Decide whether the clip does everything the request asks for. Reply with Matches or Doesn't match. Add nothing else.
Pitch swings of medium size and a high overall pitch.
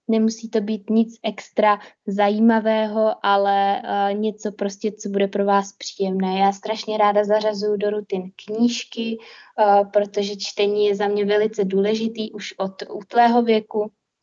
Doesn't match